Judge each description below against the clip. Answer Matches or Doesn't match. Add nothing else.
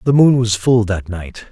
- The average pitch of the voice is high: Doesn't match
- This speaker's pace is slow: Doesn't match